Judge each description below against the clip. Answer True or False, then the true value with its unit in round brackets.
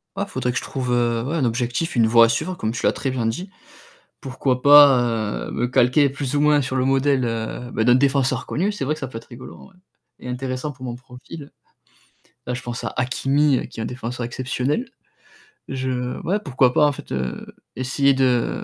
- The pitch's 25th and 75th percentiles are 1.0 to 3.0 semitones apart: True (2.4 semitones)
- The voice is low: True (130 Hz)